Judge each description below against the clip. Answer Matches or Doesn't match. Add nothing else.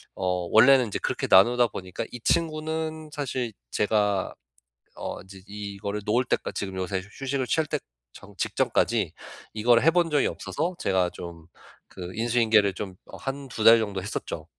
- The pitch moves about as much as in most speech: Doesn't match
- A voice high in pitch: Doesn't match